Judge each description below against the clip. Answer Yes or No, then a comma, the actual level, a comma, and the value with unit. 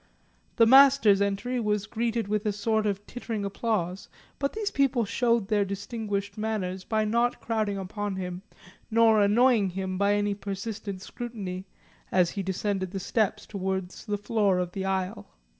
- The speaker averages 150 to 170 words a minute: Yes, average, 160 wpm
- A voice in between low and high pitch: No, high, 205 Hz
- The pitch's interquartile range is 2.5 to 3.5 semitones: Yes, average, 2.8 semitones